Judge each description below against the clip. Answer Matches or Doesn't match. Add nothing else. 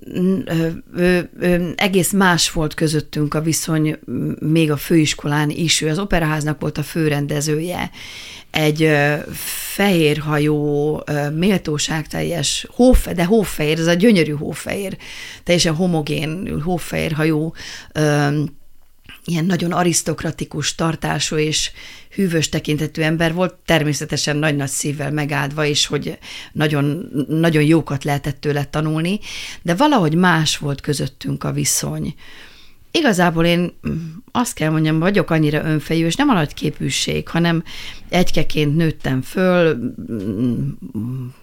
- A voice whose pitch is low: Doesn't match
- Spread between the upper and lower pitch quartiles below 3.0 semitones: Matches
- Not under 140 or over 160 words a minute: Doesn't match